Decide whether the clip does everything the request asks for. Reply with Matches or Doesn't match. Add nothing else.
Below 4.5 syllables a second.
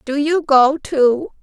Matches